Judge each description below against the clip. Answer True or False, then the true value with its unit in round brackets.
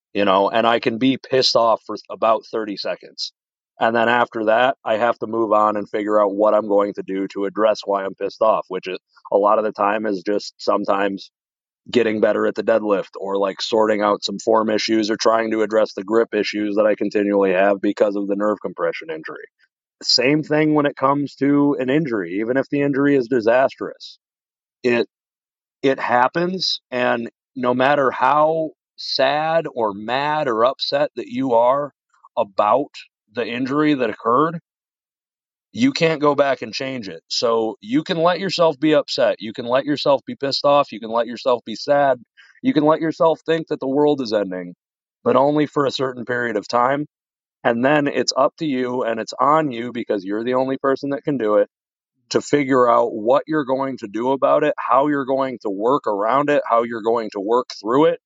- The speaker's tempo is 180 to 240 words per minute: True (200 wpm)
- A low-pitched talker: True (125 Hz)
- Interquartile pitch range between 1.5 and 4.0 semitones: False (5.3 semitones)